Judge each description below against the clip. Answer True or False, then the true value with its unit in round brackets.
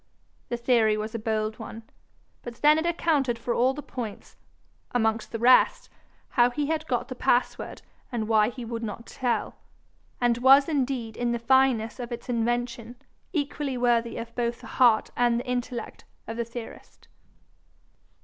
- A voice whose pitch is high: True (240 Hz)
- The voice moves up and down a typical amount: False (2.0 semitones)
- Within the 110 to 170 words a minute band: True (165 wpm)